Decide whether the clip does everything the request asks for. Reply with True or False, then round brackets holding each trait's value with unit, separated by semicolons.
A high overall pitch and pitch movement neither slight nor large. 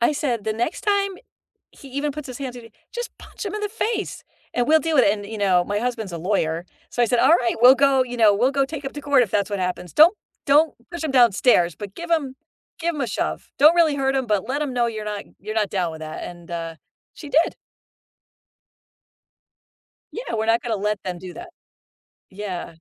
False (245 Hz; 6.3 semitones)